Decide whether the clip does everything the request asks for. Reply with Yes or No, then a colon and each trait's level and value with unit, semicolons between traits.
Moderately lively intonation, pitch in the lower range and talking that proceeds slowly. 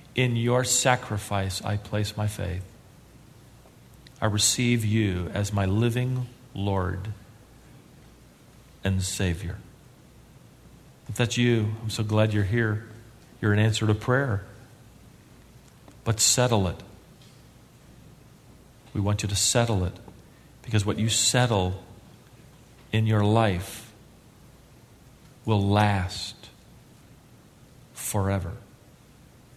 Yes: average, 3.0 semitones; low, 110 Hz; slow, 95 wpm